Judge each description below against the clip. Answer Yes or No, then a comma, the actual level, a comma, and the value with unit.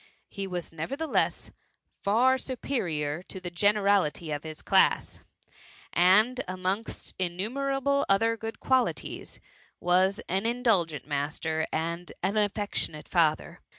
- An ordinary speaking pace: No, slow, 115 wpm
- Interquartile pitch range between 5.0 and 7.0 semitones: Yes, average, 5.3 semitones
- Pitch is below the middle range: No, high, 190 Hz